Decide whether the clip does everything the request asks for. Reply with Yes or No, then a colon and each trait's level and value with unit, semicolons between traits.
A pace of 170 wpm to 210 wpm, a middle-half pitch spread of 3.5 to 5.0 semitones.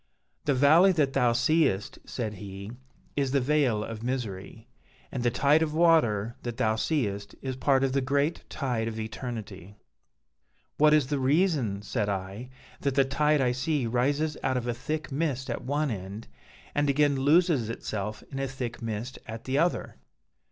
Yes: average, 175 wpm; average, 4.5 semitones